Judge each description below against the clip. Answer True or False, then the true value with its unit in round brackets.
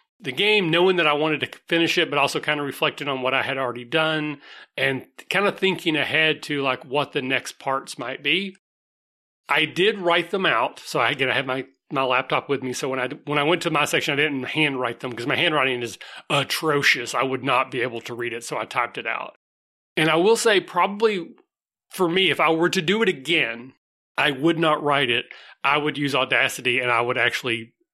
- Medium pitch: True (145 Hz)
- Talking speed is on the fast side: True (225 wpm)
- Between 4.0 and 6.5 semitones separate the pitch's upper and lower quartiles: True (4.6 semitones)